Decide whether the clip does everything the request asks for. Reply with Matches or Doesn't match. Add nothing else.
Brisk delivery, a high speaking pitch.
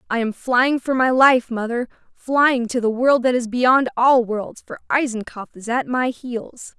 Doesn't match